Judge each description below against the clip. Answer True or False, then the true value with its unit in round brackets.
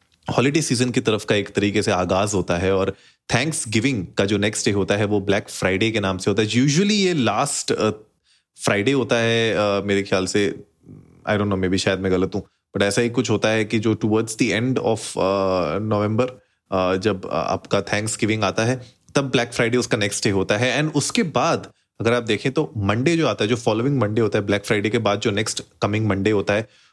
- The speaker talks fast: True (225 wpm)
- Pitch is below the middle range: True (105 Hz)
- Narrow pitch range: False (3.4 semitones)